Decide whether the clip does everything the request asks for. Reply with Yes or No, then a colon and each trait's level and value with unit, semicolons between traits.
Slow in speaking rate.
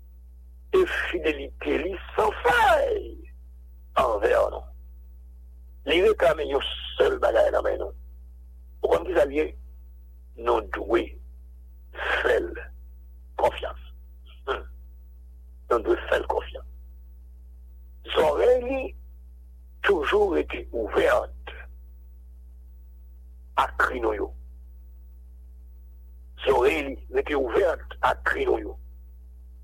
Yes: slow, 75 wpm